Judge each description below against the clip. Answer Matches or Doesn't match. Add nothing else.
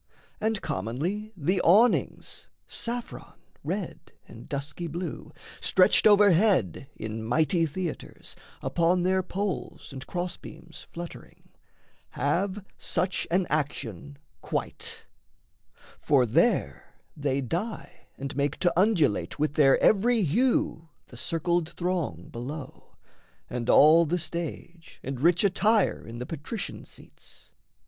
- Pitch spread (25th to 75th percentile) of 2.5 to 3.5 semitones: Doesn't match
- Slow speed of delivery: Matches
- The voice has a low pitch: Doesn't match